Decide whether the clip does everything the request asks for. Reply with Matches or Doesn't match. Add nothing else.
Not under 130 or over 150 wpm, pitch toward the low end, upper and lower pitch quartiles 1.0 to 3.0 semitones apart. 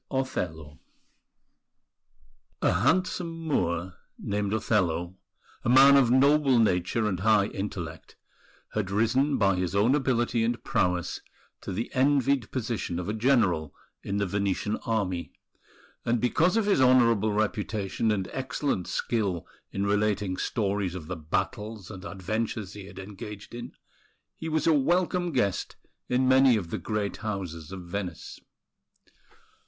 Doesn't match